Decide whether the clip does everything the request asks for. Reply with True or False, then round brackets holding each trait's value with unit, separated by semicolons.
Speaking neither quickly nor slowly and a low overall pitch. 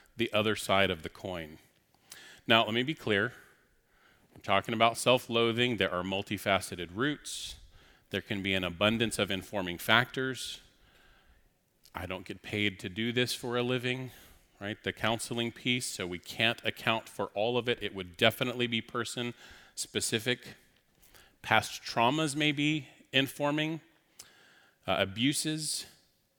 True (145 wpm; 115 Hz)